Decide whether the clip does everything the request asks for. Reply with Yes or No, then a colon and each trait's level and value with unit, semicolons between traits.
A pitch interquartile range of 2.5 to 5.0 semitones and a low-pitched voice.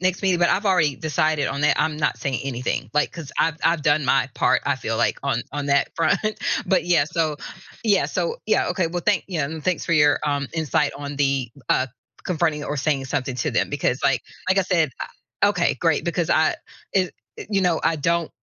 No: average, 3.5 semitones; medium, 155 Hz